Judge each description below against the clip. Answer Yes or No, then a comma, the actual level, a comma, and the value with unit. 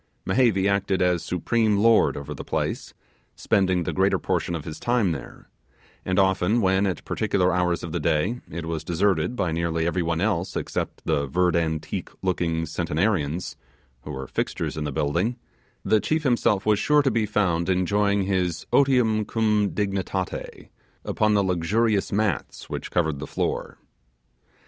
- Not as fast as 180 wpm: Yes, average, 160 wpm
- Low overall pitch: Yes, very low, 95 Hz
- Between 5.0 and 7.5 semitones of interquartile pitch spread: No, average, 4.1 semitones